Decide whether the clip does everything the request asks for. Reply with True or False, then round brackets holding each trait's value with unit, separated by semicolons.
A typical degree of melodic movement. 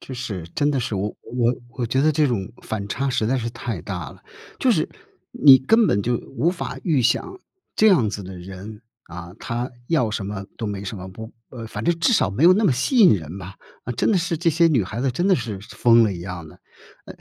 False (6.6 semitones)